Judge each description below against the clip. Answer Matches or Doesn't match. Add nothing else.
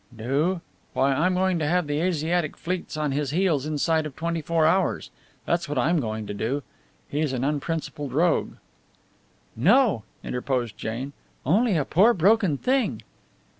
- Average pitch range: Matches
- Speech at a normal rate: Matches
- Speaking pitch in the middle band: Matches